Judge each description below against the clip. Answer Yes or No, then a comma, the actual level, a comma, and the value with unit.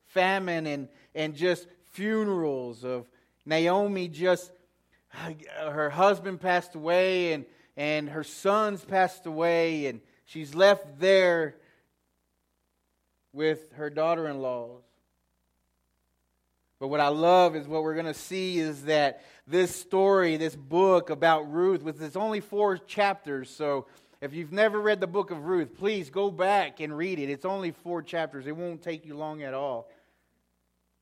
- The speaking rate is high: No, average, 145 wpm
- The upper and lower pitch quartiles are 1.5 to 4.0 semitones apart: No, average, 4.6 semitones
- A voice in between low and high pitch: Yes, medium, 160 Hz